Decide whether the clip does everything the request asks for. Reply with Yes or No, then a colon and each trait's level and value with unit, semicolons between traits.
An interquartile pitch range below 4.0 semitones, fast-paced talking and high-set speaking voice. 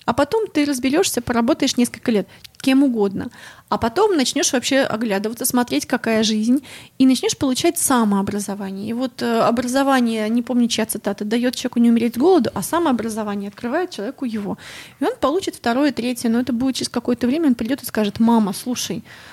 Yes: average, 3.5 semitones; fast, 175 wpm; high, 245 Hz